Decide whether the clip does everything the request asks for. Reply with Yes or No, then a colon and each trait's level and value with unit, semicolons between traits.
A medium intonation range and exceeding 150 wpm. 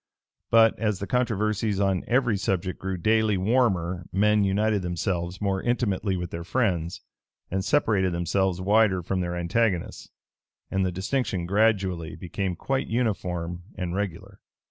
No: average, 3.4 semitones; average, 140 wpm